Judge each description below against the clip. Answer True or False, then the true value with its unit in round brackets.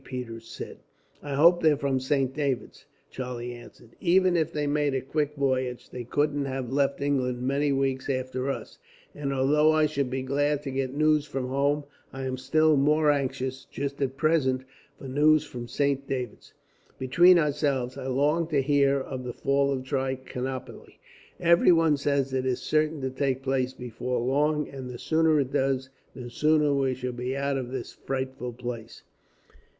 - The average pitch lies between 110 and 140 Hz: True (135 Hz)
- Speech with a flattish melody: True (2.2 semitones)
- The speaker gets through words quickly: False (175 wpm)